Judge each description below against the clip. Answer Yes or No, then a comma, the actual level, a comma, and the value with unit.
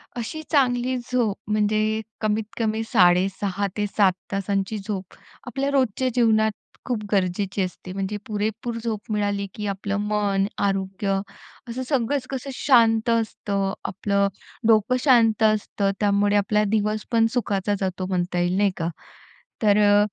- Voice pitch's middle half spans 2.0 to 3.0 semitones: Yes, narrow, 2.4 semitones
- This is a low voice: No, high, 210 Hz